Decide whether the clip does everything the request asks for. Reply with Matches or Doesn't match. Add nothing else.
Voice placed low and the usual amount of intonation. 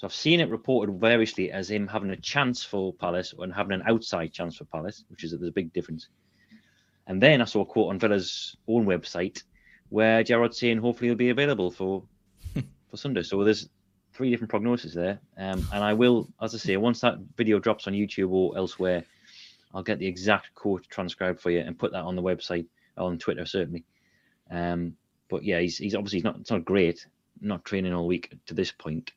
Matches